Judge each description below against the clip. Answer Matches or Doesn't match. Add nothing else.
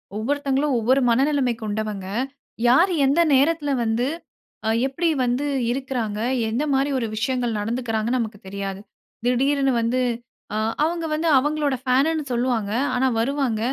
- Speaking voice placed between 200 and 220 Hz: Doesn't match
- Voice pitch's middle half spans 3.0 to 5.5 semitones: Matches